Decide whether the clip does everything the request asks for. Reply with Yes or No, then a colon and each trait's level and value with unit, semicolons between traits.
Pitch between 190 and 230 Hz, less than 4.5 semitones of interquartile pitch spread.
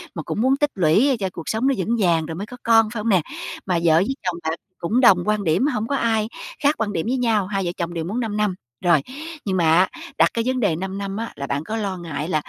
No: high, 200 Hz; average, 5.0 semitones